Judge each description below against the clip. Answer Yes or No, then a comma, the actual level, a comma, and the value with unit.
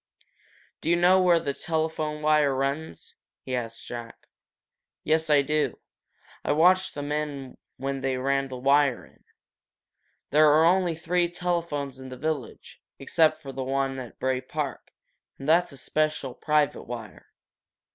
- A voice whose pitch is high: No, medium, 145 Hz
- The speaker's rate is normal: Yes, average, 155 wpm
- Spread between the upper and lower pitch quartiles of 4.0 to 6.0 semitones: No, average, 3.0 semitones